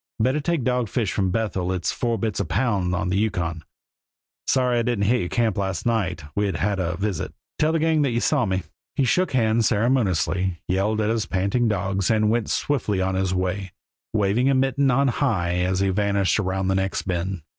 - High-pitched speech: No, low, 105 Hz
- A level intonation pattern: No, average, 4.2 semitones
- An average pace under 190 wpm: No, fast, 205 wpm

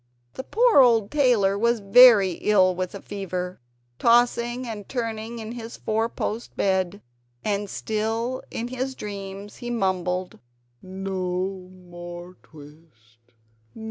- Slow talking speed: Yes, slow, 120 wpm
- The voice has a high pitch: Yes, high, 205 Hz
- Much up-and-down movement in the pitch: No, average, 4.2 semitones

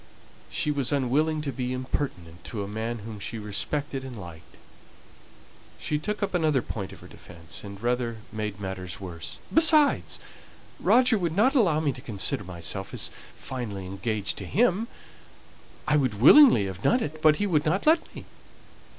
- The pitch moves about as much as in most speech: No, wide, 7.6 semitones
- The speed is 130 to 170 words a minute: Yes, average, 165 wpm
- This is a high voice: No, low, 125 Hz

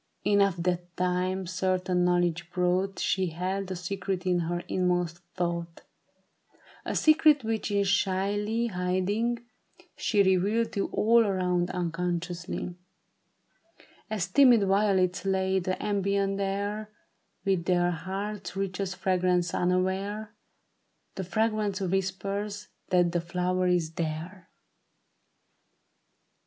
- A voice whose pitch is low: No, medium, 185 Hz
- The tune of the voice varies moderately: No, narrow, 2.1 semitones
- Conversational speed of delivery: No, slow, 110 wpm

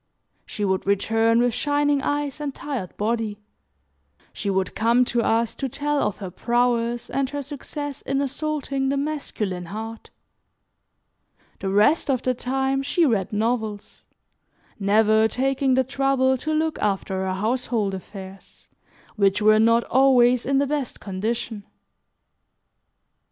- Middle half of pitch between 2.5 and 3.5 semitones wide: No, average, 4.5 semitones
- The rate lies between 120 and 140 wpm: Yes, slow, 135 wpm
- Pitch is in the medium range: No, high, 240 Hz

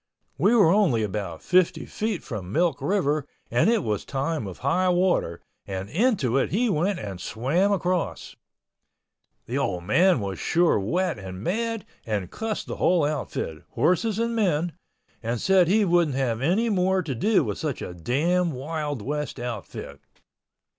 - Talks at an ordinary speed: Yes, average, 155 wpm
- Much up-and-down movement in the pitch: Yes, wide, 8.5 semitones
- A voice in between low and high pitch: Yes, medium, 155 Hz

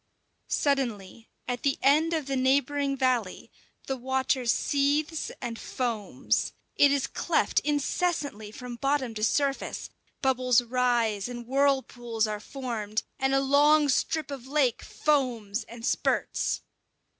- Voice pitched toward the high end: Yes, very high, 260 Hz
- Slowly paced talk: Yes, slow, 125 wpm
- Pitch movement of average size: Yes, average, 3.2 semitones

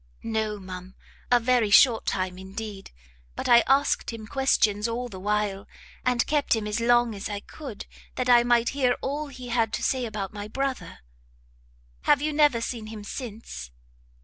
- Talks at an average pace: Yes, average, 175 wpm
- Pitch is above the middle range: Yes, high, 230 Hz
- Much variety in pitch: No, average, 3.3 semitones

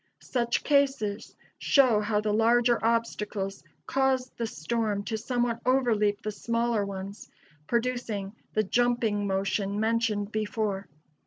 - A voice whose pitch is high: Yes, high, 220 Hz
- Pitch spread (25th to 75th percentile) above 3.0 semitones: No, average, 2.7 semitones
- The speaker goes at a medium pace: No, slow, 115 wpm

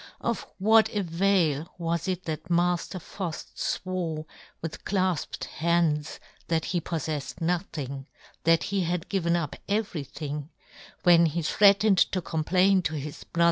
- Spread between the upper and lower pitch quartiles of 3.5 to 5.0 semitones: No, average, 2.9 semitones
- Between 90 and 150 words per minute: Yes, average, 145 wpm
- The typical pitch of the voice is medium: Yes, medium, 170 Hz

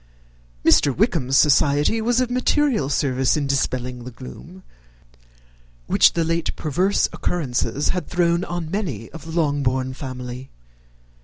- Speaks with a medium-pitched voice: Yes, medium, 145 Hz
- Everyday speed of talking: No, slow, 130 wpm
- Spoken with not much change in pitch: No, average, 5.3 semitones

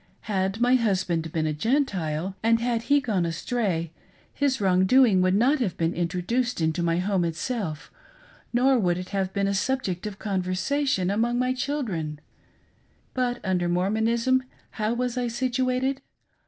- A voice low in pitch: No, high, 205 Hz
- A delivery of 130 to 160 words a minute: Yes, average, 155 wpm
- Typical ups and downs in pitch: No, wide, 5.7 semitones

